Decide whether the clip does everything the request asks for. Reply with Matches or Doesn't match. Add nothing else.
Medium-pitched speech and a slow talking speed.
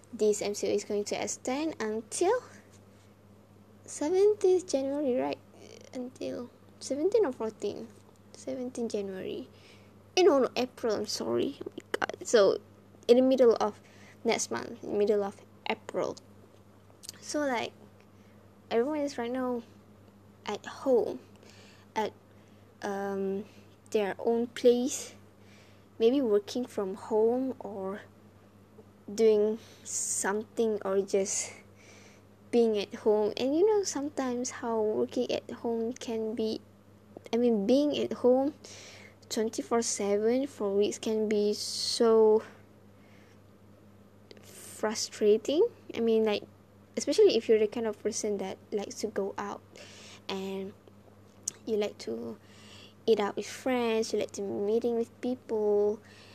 Doesn't match